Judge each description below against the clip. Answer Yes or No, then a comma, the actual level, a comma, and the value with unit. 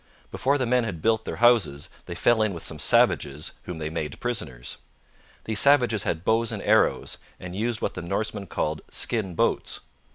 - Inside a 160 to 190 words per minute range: Yes, average, 185 wpm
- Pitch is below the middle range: Yes, low, 105 Hz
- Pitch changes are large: Yes, wide, 6.4 semitones